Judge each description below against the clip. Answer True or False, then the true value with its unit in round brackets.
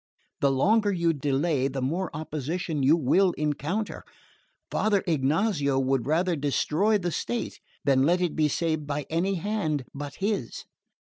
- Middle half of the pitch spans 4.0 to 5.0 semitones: True (4.6 semitones)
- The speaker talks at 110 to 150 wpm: True (145 wpm)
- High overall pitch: False (155 Hz)